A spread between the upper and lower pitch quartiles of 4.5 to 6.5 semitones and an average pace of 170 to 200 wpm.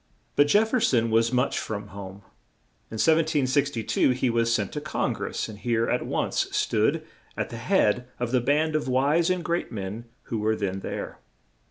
Yes: average, 5.2 semitones; average, 190 wpm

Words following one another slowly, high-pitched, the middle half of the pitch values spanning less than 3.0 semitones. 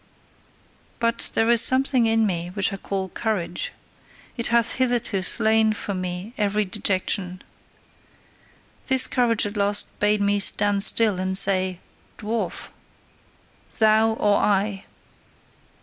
Yes: slow, 120 wpm; high, 205 Hz; narrow, 2.6 semitones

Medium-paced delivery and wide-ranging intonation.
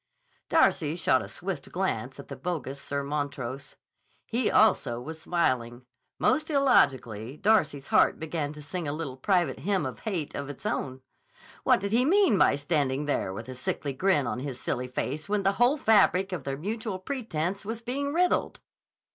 Yes: average, 175 wpm; wide, 7.4 semitones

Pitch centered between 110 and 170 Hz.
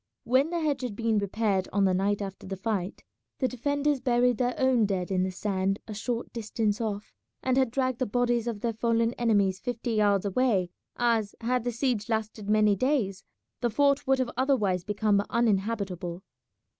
No: high, 225 Hz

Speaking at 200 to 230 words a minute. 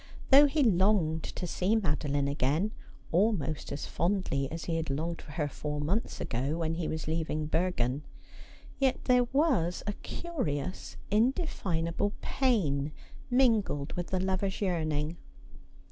No: slow, 135 wpm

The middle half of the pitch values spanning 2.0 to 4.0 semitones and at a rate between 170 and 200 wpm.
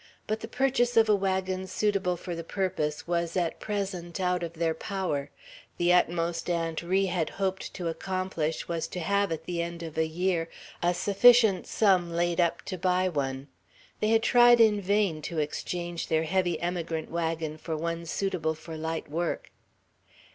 Yes: average, 2.7 semitones; average, 175 wpm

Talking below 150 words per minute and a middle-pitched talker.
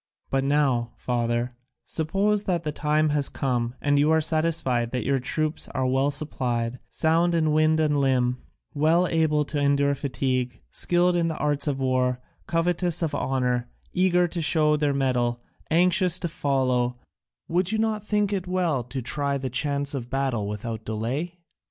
No: average, 165 wpm; medium, 145 Hz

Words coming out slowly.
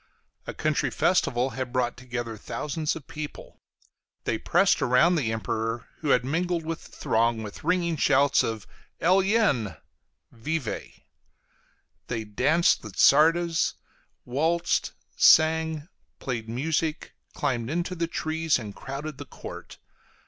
Yes: slow, 125 wpm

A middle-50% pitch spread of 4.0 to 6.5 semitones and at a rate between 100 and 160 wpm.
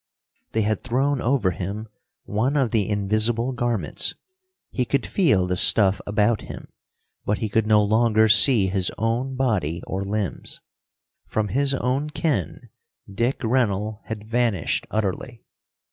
No: average, 3.4 semitones; average, 140 wpm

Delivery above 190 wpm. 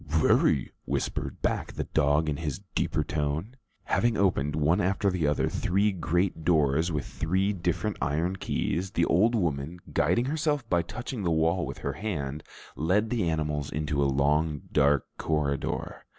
No: average, 160 wpm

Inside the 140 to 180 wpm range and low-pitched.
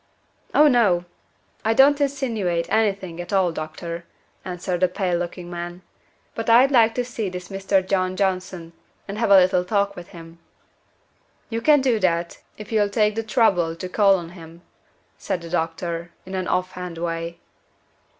No: average, 170 wpm; medium, 185 Hz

